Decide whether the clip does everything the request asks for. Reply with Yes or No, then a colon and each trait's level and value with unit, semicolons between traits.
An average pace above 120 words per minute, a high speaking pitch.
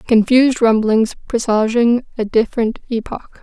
No: slow, 105 wpm; high, 230 Hz